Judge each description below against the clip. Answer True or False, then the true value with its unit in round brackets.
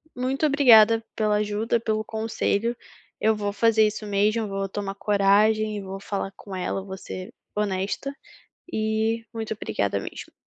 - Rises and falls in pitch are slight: True (2.0 semitones)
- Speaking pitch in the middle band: False (215 Hz)